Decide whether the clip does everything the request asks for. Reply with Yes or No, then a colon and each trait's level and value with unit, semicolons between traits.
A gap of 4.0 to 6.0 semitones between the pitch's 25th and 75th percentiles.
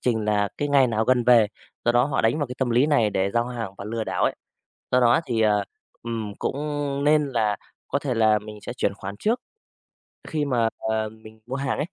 No: average, 3.4 semitones